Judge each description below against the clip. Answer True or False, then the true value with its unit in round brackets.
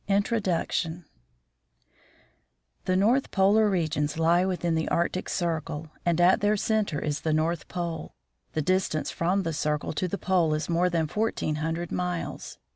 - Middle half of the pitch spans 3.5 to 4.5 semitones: False (2.9 semitones)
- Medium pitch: True (170 Hz)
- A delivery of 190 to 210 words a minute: False (150 wpm)